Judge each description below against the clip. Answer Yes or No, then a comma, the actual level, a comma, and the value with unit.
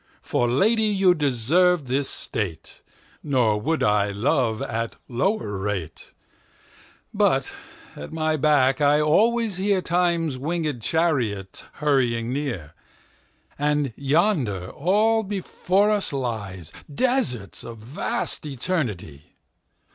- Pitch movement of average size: No, wide, 7.5 semitones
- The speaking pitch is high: No, medium, 140 Hz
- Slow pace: Yes, slow, 90 wpm